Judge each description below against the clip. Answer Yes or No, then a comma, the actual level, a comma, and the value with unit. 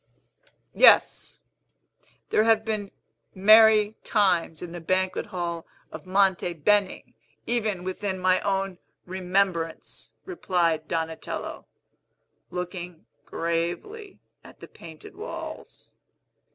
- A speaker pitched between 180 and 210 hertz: Yes, medium, 185 Hz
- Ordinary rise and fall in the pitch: Yes, average, 3.3 semitones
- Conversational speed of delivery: No, slow, 95 wpm